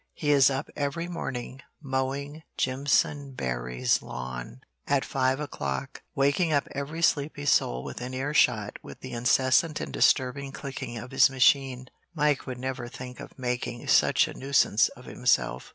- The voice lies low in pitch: Yes, low, 130 Hz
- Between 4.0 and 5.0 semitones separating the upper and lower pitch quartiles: No, narrow, 2.5 semitones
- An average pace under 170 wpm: Yes, average, 150 wpm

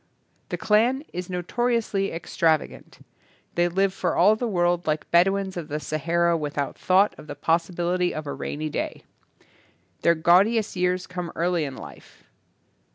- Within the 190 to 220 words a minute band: No, average, 155 wpm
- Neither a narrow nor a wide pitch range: Yes, average, 3.0 semitones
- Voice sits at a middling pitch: Yes, medium, 175 Hz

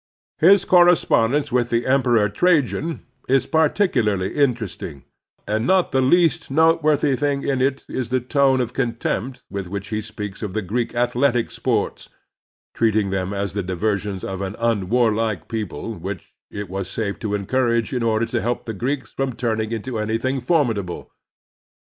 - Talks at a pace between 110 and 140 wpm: No, average, 160 wpm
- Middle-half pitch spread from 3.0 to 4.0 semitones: No, average, 4.5 semitones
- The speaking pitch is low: Yes, low, 115 Hz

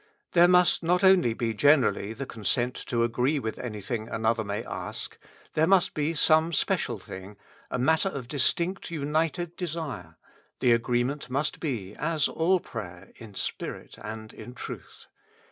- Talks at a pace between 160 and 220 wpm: No, average, 145 wpm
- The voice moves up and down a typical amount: No, wide, 6.2 semitones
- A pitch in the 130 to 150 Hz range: Yes, low, 135 Hz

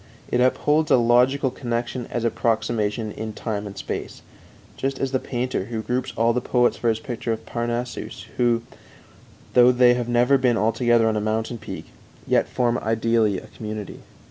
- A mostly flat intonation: Yes, narrow, 1.8 semitones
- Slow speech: No, average, 175 wpm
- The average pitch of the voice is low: Yes, low, 120 Hz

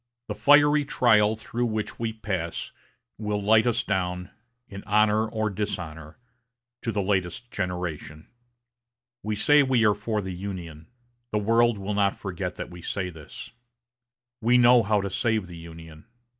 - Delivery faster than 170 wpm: No, average, 155 wpm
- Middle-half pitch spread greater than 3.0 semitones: Yes, average, 3.7 semitones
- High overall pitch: No, low, 105 Hz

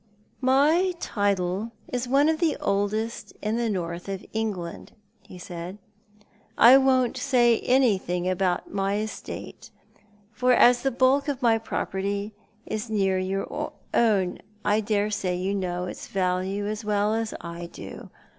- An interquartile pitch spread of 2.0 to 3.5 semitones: No, average, 4.0 semitones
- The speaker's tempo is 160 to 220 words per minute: No, average, 150 wpm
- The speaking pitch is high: Yes, high, 210 Hz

